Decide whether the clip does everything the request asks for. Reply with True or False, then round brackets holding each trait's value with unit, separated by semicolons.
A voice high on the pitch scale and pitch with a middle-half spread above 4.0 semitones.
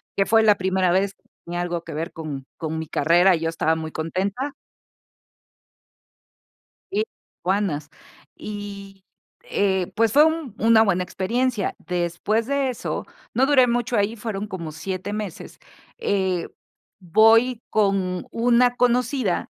True (200 Hz; 4.6 semitones)